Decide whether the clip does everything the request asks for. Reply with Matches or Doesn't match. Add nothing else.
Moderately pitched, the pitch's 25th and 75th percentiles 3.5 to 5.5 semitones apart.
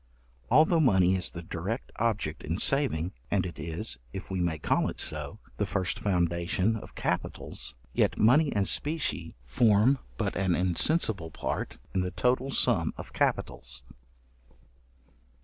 Doesn't match